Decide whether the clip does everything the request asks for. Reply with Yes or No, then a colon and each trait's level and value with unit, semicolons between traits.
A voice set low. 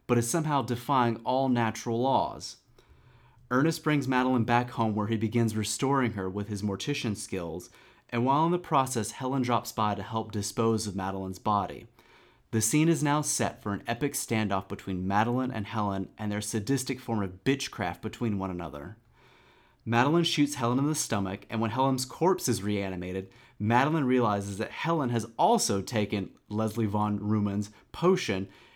Yes: low, 115 Hz